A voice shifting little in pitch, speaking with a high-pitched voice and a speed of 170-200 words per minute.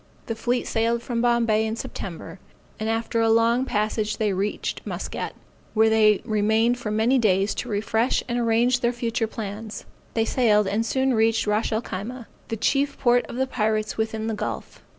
Yes: narrow, 1.8 semitones; high, 225 Hz; average, 180 wpm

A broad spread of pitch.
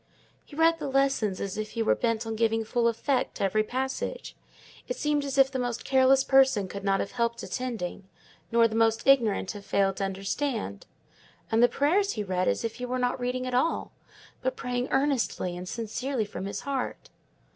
No: average, 4.0 semitones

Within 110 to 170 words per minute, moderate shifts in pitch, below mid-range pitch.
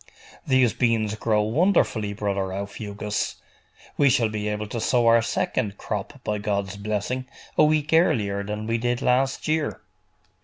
Yes: average, 150 wpm; average, 3.4 semitones; low, 110 Hz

